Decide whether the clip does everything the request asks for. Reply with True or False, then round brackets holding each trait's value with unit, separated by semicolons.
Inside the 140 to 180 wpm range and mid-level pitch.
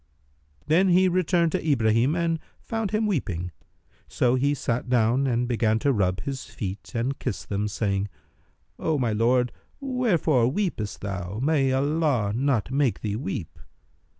False (150 wpm; 130 Hz)